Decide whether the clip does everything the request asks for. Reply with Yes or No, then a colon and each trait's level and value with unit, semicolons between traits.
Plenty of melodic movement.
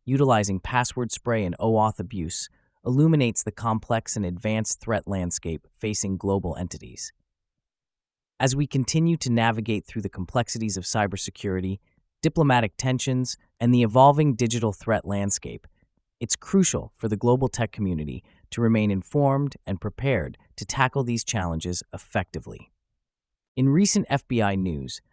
No: average, 4.7 semitones